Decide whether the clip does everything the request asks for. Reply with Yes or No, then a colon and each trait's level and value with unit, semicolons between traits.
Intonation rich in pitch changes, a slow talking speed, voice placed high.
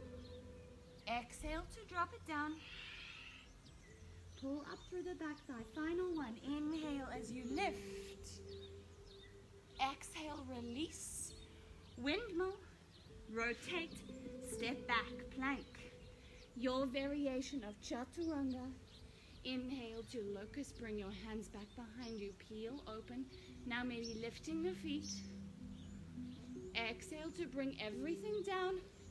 Yes: wide, 6.9 semitones; slow, 100 wpm; high, 245 Hz